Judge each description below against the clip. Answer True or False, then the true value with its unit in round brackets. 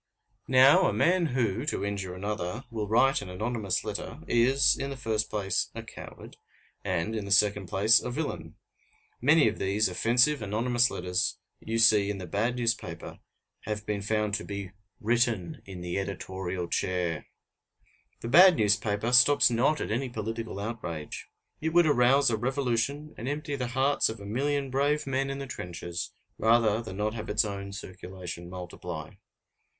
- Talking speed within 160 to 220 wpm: True (165 wpm)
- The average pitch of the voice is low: True (110 Hz)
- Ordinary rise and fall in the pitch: True (4.4 semitones)